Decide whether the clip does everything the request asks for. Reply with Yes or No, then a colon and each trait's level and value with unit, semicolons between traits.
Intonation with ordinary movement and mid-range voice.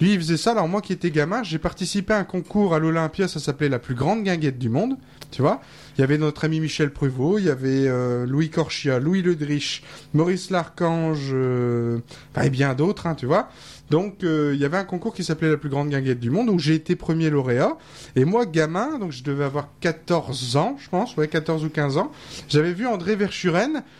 Yes: average, 4.3 semitones; medium, 160 Hz